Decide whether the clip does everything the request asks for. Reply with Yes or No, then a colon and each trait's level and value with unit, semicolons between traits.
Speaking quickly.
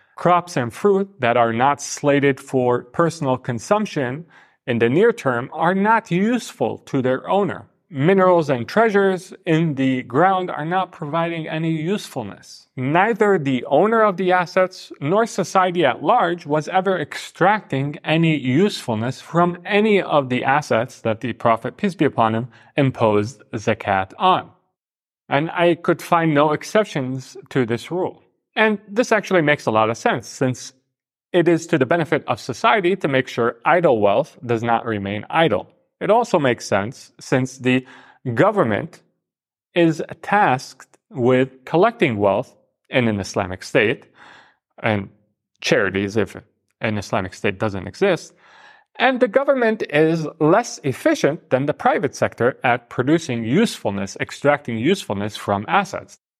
No: average, 145 wpm